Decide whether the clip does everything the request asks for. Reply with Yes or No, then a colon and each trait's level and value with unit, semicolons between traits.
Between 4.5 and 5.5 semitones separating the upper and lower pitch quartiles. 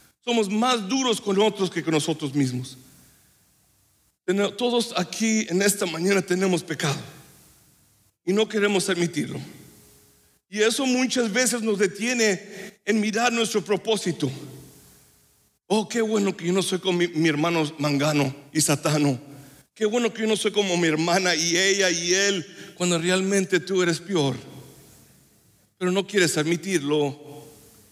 Yes: average, 5.2 semitones